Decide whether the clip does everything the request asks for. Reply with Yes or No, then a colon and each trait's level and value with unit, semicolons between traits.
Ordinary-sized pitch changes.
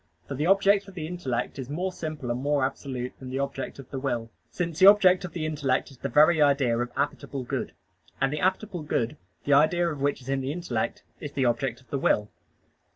Yes: average, 4.3 semitones